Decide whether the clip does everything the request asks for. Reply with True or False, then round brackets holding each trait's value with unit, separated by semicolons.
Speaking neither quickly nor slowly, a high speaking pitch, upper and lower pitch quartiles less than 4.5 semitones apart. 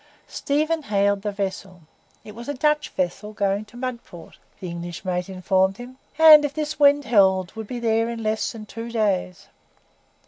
False (175 wpm; 215 Hz; 5.0 semitones)